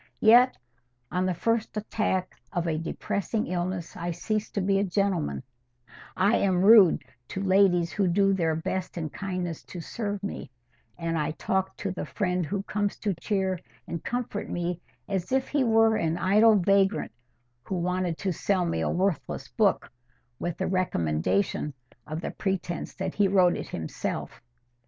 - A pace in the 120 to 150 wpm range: No, average, 165 wpm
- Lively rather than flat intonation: No, average, 2.7 semitones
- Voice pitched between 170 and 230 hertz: Yes, medium, 185 Hz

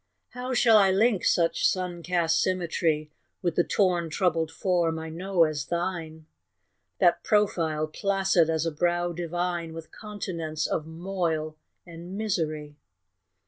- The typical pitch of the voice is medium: Yes, medium, 170 Hz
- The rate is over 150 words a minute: No, slow, 135 wpm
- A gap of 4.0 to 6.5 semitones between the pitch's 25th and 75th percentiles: No, narrow, 2.5 semitones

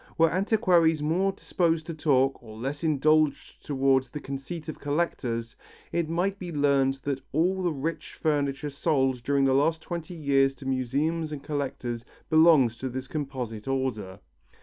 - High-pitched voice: No, medium, 145 Hz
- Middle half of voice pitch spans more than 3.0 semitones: Yes, average, 3.4 semitones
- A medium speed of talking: Yes, average, 155 wpm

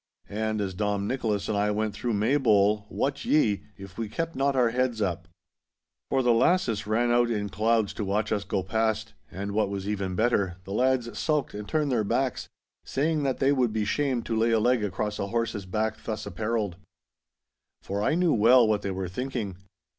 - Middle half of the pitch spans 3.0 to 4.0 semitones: Yes, average, 3.3 semitones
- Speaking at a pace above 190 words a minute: Yes, average, 200 wpm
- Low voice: Yes, low, 110 Hz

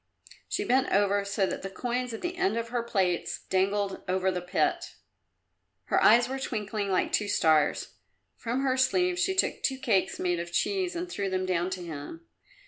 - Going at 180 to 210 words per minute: Yes, average, 190 wpm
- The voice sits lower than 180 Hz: No, high, 205 Hz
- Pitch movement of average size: No, wide, 5.8 semitones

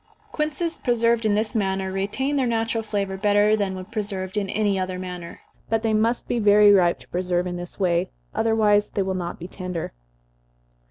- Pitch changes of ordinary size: Yes, average, 3.1 semitones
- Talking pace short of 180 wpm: No, average, 185 wpm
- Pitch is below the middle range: No, high, 205 Hz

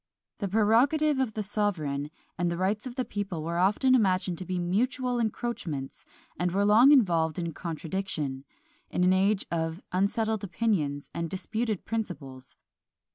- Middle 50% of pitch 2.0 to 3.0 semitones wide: No, average, 4.7 semitones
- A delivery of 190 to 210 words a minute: No, average, 150 wpm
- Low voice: No, high, 190 Hz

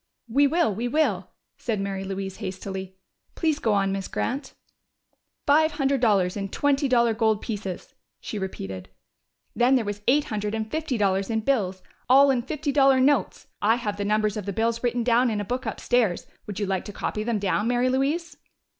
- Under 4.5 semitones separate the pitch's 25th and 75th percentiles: No, average, 4.8 semitones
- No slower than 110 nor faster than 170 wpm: No, average, 190 wpm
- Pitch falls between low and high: No, high, 225 Hz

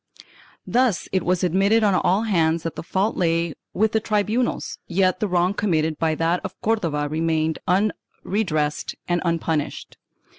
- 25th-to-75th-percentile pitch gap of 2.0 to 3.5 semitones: No, average, 4.2 semitones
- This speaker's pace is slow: No, average, 155 wpm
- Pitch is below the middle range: No, medium, 180 Hz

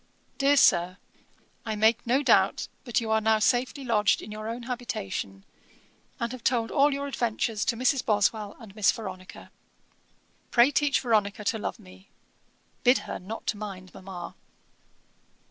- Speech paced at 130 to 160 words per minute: Yes, average, 150 wpm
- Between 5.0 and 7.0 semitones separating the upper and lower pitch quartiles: No, average, 3.3 semitones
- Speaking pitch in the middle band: No, high, 220 Hz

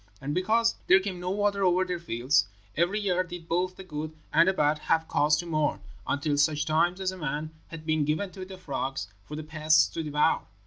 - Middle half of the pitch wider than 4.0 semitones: No, average, 3.5 semitones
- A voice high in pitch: No, medium, 165 Hz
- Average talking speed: No, fast, 220 wpm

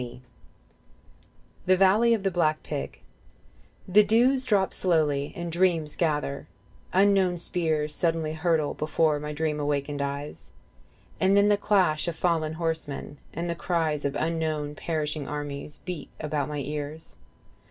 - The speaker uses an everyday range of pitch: Yes, average, 3.3 semitones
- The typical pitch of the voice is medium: Yes, medium, 160 Hz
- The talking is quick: No, average, 140 wpm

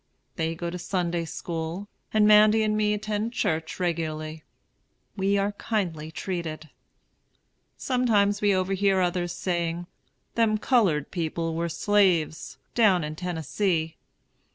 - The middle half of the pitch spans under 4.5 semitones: Yes, average, 4.1 semitones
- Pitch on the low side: No, medium, 180 Hz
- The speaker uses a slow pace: Yes, slow, 120 wpm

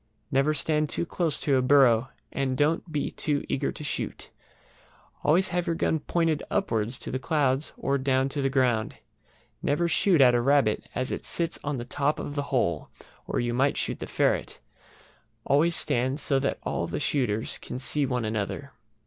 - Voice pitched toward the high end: No, medium, 140 Hz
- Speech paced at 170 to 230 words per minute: Yes, average, 185 wpm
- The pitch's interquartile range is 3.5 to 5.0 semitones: No, average, 3.1 semitones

